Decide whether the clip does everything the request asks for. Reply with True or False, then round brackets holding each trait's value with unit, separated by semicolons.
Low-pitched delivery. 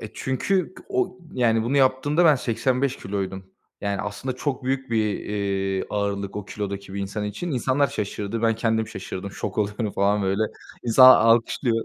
True (110 Hz)